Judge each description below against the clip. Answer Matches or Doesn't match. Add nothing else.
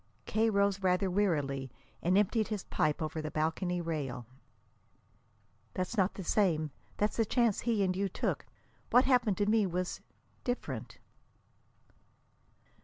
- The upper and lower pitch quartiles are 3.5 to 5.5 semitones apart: Matches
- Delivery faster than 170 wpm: Doesn't match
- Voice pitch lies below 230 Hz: Matches